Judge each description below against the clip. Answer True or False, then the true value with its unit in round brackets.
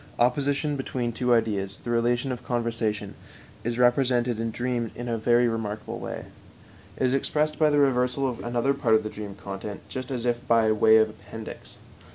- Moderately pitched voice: False (120 Hz)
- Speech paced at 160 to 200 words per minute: True (185 wpm)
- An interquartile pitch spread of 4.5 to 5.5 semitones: False (2.4 semitones)